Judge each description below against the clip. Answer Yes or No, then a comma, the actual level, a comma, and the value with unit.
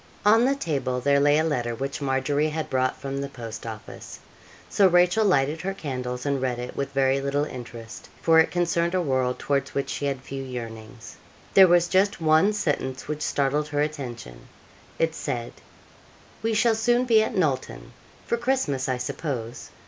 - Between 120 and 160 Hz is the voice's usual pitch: Yes, medium, 140 Hz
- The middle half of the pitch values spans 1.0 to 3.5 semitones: No, average, 4.9 semitones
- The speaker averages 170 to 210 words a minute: Yes, average, 180 wpm